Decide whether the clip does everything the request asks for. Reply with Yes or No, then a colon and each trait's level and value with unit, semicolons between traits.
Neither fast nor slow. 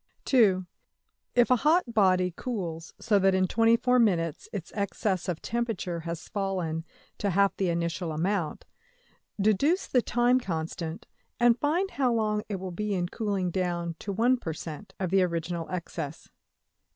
Yes: average, 145 wpm